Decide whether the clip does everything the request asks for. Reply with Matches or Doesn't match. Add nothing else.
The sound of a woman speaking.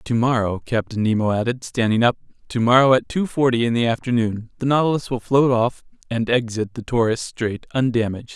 Doesn't match